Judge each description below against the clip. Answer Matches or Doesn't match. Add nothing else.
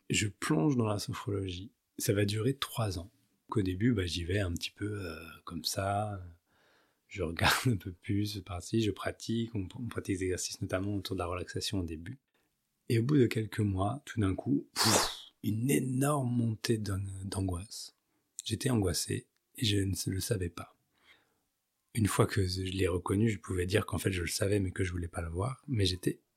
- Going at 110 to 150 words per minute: Doesn't match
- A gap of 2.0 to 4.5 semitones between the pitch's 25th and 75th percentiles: Matches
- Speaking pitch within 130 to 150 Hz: Doesn't match